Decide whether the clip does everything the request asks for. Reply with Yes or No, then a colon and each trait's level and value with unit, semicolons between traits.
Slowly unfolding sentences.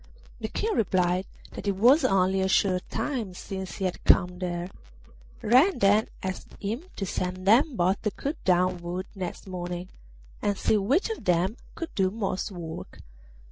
No: average, 170 wpm